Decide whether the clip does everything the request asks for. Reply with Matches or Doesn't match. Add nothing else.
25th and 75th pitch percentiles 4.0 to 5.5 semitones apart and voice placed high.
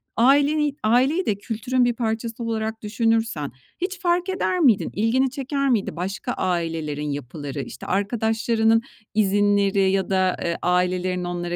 Matches